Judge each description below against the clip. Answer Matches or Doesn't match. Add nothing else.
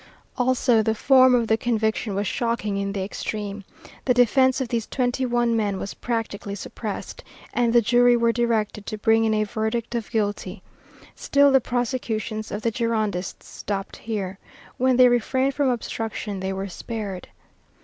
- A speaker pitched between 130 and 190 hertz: Doesn't match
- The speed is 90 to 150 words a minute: Doesn't match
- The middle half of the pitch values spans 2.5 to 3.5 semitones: Matches